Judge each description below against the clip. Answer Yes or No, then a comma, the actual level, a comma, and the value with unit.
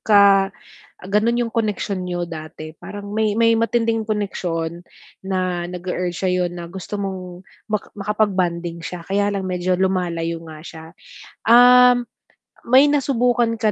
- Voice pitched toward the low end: No, high, 195 Hz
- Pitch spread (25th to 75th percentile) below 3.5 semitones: No, average, 4.0 semitones